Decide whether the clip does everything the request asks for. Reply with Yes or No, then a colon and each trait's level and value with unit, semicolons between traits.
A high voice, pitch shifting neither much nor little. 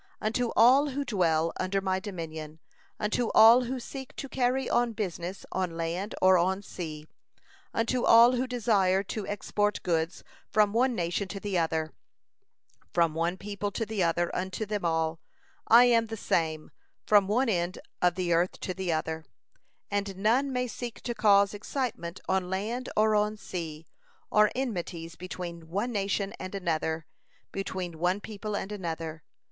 Yes: high, 195 Hz; average, 4.5 semitones